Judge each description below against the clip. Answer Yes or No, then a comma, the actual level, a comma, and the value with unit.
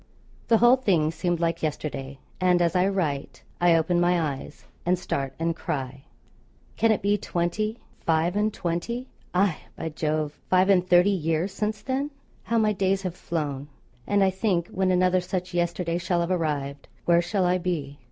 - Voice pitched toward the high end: No, medium, 175 Hz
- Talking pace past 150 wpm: Yes, average, 175 wpm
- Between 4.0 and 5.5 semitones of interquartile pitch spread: No, average, 3.0 semitones